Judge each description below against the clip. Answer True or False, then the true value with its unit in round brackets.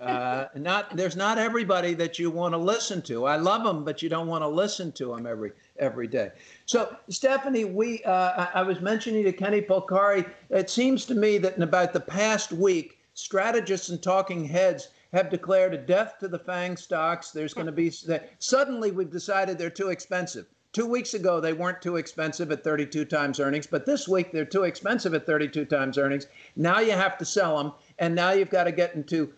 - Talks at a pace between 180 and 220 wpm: True (205 wpm)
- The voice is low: False (180 Hz)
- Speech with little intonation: False (3.8 semitones)